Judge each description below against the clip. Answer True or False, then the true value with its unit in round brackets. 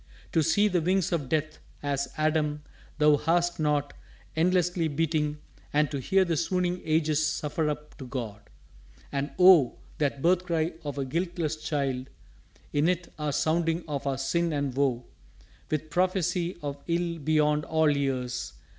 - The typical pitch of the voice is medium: True (155 Hz)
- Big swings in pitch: False (2.9 semitones)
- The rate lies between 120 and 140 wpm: False (155 wpm)